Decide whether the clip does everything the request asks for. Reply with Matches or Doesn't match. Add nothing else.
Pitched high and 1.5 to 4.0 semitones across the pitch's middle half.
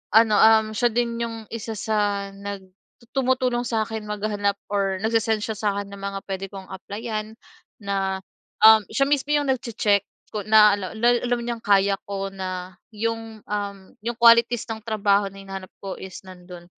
Matches